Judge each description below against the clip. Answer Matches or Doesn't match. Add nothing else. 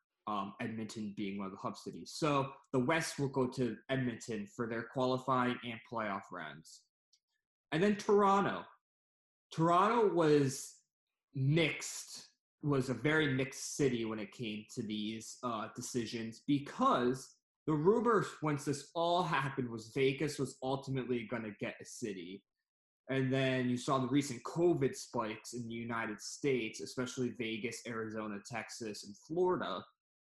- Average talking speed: Matches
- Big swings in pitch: Doesn't match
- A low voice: Matches